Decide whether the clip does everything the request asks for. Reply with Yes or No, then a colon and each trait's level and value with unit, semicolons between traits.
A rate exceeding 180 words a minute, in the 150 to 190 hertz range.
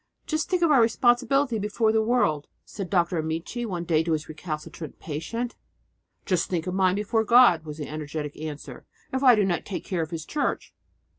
Yes: average, 195 wpm; medium, 185 Hz